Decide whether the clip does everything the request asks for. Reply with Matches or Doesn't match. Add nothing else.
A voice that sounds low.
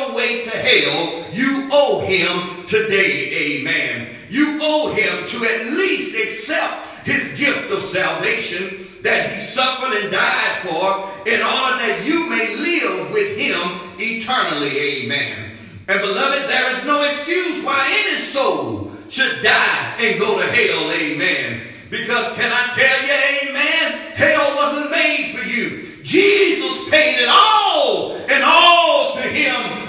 Doesn't match